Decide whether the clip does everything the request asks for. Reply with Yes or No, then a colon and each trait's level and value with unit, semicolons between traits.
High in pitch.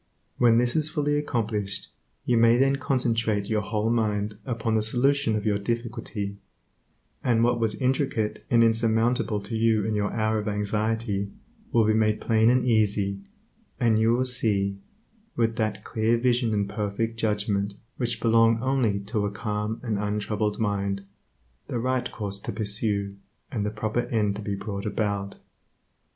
No: low, 110 Hz